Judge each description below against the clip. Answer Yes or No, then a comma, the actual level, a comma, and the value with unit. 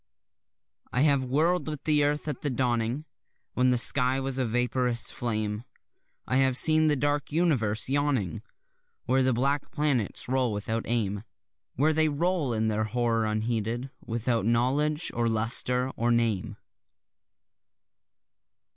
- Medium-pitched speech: No, low, 125 Hz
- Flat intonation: No, average, 4.0 semitones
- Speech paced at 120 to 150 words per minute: Yes, average, 140 wpm